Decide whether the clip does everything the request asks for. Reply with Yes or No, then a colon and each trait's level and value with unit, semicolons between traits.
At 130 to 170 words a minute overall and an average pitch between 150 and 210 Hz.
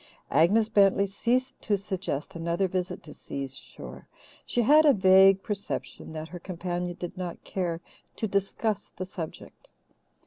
Yes: average, 145 wpm; high, 190 Hz